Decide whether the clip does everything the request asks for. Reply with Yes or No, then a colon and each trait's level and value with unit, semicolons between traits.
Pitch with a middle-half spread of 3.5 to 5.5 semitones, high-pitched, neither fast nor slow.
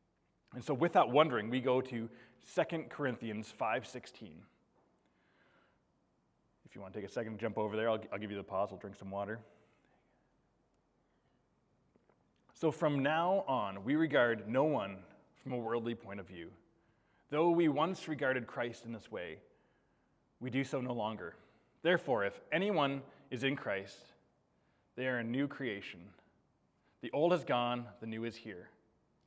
No: average, 4.3 semitones; low, 120 Hz; average, 160 wpm